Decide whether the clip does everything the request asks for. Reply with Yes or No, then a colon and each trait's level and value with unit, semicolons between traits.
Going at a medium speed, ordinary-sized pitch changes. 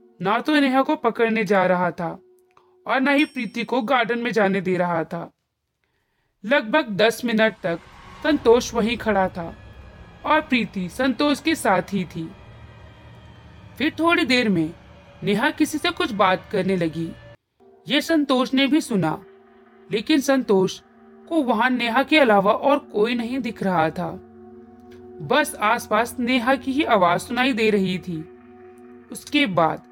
No: average, 150 wpm; wide, 7.9 semitones